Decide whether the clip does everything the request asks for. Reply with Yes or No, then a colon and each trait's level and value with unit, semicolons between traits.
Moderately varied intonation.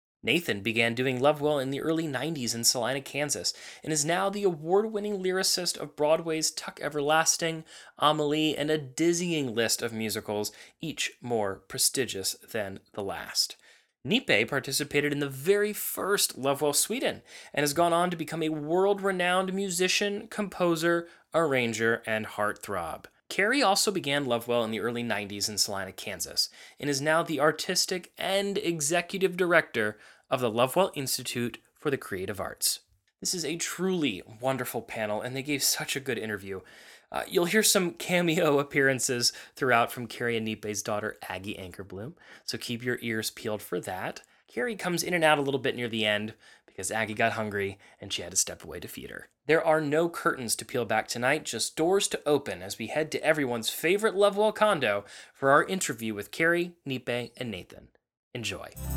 No: wide, 6.8 semitones